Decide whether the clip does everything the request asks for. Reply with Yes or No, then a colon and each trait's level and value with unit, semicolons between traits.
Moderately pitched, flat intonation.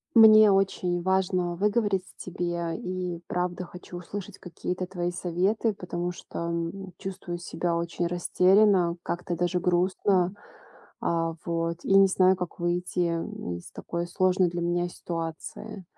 Yes: medium, 180 Hz; narrow, 1.5 semitones